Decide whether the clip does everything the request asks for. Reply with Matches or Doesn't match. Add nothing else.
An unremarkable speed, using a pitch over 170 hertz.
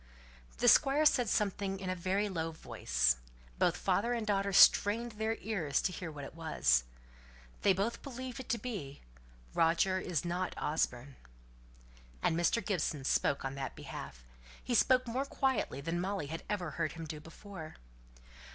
Matches